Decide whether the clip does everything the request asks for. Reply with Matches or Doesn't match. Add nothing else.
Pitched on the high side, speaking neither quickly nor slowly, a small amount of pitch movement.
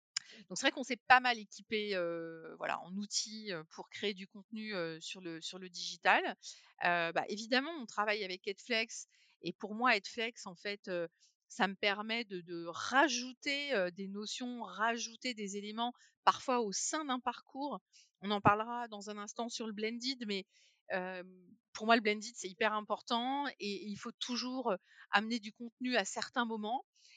Doesn't match